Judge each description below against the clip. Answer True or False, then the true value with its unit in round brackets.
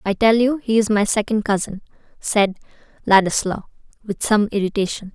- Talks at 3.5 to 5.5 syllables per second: True (5.4 syllables/s)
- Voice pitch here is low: False (210 Hz)